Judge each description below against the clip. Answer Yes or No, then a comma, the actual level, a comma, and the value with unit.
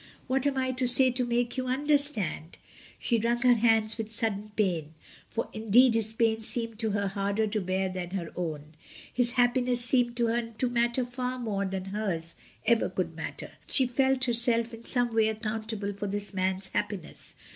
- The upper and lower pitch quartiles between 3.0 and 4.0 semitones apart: Yes, average, 3.4 semitones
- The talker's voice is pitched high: Yes, high, 225 Hz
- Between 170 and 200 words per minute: Yes, average, 190 wpm